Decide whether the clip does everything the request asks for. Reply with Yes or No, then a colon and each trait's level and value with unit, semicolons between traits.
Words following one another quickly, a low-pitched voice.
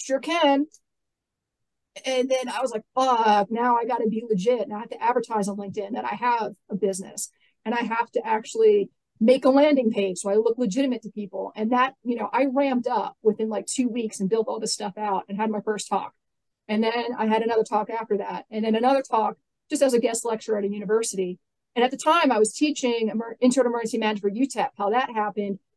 No: fast, 230 wpm; high, 225 Hz